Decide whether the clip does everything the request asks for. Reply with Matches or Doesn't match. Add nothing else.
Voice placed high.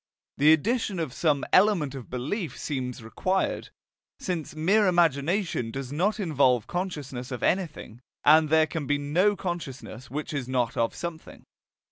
Doesn't match